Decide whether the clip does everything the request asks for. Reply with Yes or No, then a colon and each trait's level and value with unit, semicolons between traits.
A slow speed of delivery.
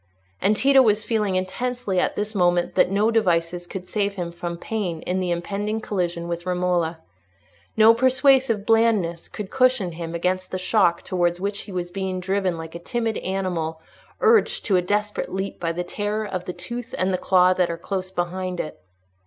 No: average, 185 wpm